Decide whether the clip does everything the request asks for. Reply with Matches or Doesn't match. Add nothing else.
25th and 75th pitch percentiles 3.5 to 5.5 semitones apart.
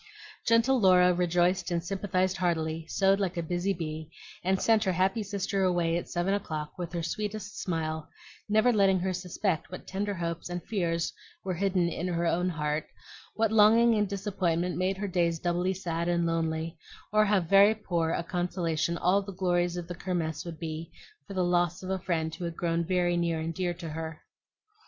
Doesn't match